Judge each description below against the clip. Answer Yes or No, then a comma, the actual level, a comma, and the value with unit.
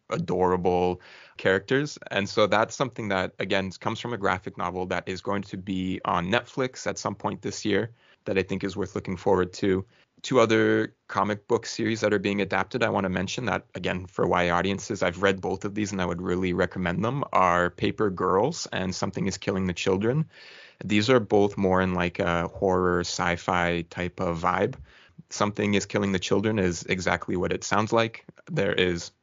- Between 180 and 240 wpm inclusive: Yes, average, 195 wpm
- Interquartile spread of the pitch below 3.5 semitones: Yes, narrow, 2.4 semitones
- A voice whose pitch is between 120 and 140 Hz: No, very low, 95 Hz